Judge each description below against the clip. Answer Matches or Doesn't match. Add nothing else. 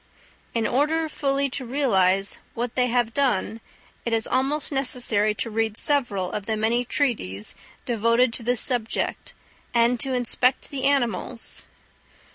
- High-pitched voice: Matches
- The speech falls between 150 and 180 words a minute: Doesn't match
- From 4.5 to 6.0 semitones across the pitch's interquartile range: Doesn't match